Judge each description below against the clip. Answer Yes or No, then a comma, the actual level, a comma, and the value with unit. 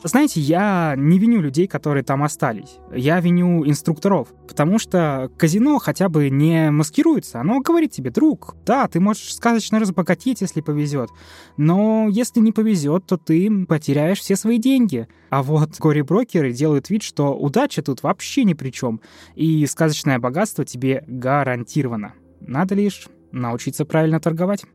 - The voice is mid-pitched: Yes, medium, 160 Hz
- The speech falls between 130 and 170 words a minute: Yes, average, 150 wpm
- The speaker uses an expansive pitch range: Yes, wide, 6.2 semitones